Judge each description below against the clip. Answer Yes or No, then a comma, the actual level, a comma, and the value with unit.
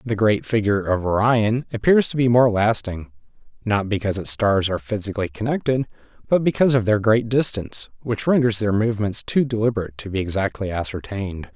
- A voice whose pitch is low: Yes, low, 110 Hz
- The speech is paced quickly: No, average, 170 wpm